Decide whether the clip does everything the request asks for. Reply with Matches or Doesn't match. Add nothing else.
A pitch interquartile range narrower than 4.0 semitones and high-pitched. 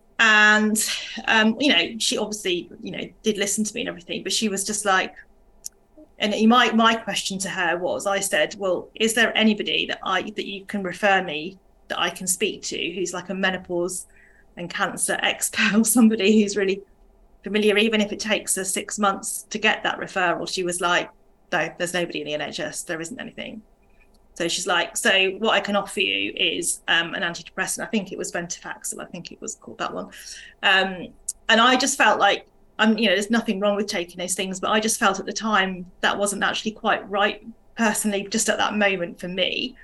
Matches